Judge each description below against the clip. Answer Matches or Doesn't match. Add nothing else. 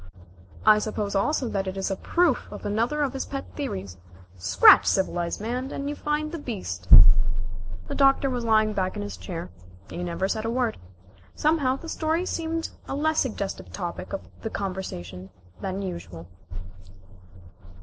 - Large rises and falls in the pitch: Matches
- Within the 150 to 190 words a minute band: Matches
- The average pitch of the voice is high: Matches